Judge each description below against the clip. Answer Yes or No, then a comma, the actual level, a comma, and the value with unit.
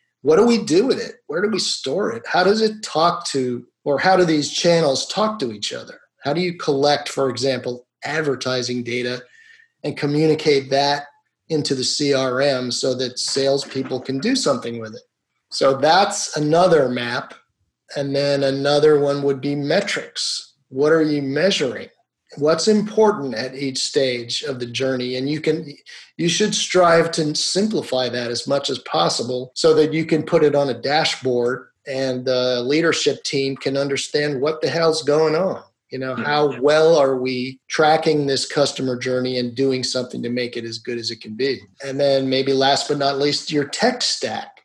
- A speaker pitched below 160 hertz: Yes, medium, 140 Hz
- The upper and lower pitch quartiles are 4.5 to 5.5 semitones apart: No, average, 3.5 semitones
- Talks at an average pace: Yes, average, 180 wpm